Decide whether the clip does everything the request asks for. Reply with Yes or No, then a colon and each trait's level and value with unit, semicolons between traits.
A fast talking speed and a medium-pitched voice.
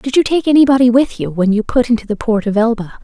No: fast, 275 wpm; high, 235 Hz